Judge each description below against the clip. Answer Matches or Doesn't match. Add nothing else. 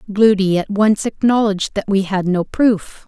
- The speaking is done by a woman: Matches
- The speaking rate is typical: Matches